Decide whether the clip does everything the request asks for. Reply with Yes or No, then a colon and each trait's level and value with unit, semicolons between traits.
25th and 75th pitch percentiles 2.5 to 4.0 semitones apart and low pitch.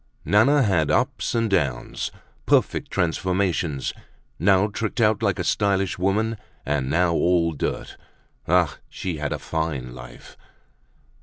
No: average, 4.4 semitones; very low, 90 Hz